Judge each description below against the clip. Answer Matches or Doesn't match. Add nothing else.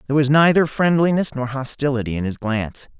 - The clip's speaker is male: Matches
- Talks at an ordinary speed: Matches